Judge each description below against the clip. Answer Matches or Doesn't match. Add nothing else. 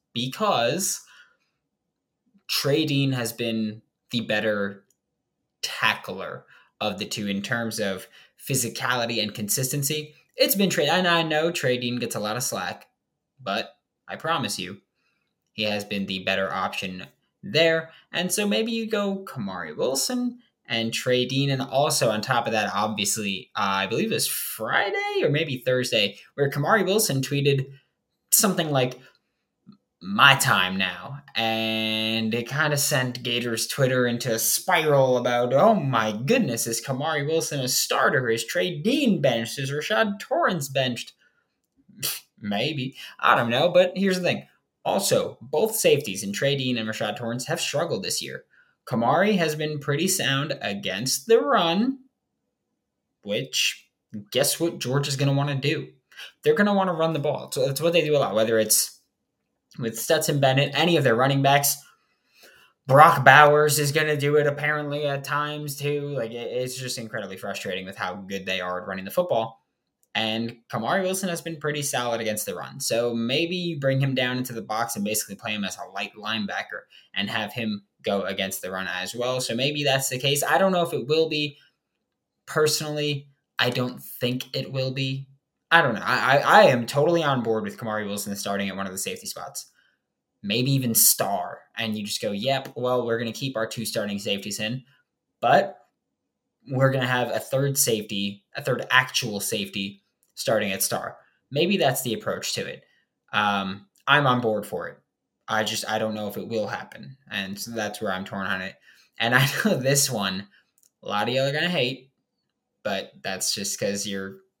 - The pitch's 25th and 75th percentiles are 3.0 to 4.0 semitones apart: Doesn't match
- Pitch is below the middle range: Matches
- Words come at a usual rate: Matches